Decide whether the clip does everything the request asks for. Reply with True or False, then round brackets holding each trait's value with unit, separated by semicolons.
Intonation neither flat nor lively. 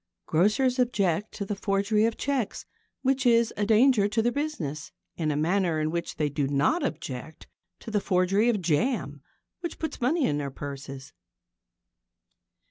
False (7.7 semitones)